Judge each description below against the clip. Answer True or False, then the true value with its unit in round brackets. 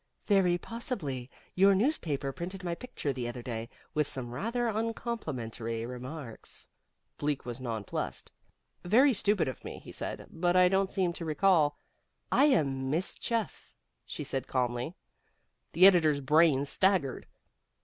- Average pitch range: False (6.9 semitones)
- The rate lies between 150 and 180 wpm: False (140 wpm)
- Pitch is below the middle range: False (160 Hz)